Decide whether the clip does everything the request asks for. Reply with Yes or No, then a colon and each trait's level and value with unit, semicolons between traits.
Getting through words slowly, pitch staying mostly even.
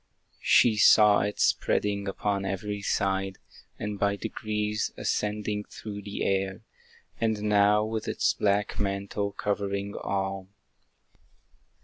Yes: slow, 110 wpm; narrow, 1.1 semitones